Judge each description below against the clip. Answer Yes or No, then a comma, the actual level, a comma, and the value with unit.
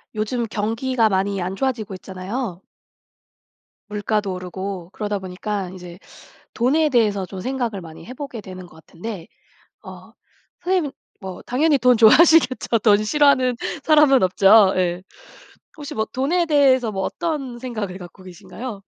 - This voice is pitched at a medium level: No, high, 215 Hz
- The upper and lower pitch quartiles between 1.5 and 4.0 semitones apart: No, wide, 5.4 semitones